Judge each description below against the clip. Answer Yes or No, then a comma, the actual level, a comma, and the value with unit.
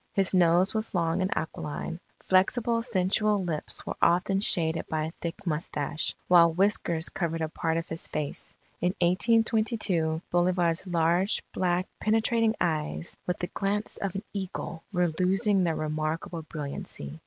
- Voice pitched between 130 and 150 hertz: No, medium, 175 Hz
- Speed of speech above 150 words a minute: No, average, 145 wpm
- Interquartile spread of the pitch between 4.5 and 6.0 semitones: No, average, 3.1 semitones